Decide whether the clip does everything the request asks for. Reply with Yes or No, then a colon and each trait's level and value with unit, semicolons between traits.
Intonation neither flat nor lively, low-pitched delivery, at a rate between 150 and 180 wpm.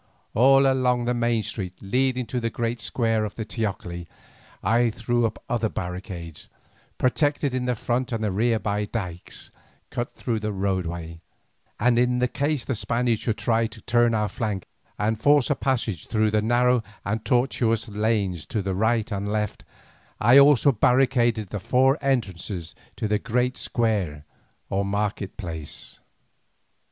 Yes: average, 3.3 semitones; low, 115 Hz; average, 155 wpm